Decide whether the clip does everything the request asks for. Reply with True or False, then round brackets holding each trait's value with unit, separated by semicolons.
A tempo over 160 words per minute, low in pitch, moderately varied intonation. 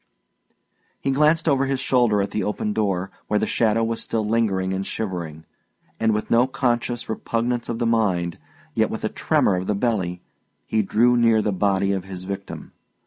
True (185 wpm; 110 Hz; 3.5 semitones)